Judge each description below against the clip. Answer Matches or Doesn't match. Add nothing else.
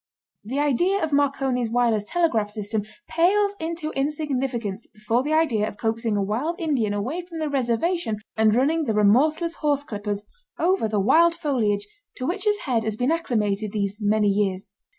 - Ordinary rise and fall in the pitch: Doesn't match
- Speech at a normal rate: Matches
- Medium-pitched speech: Doesn't match